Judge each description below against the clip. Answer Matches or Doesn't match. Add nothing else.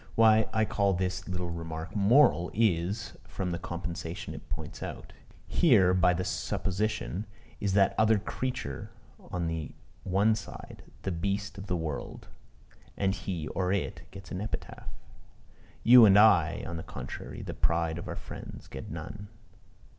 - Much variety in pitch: Doesn't match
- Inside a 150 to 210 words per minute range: Matches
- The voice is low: Matches